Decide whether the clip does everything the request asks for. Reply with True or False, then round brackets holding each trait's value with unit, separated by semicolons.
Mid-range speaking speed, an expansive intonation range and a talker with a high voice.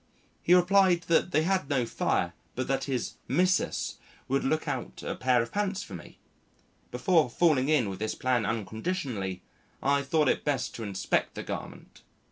False (170 wpm; 6.6 semitones; 135 Hz)